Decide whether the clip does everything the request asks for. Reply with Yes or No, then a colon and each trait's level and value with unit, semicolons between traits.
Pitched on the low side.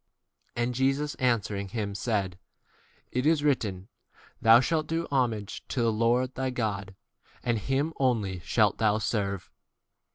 Yes: low, 115 Hz